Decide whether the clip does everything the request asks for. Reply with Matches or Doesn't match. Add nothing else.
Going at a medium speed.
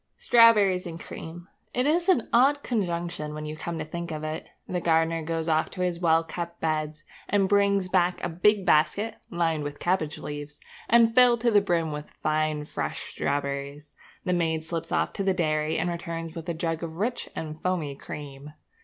Matches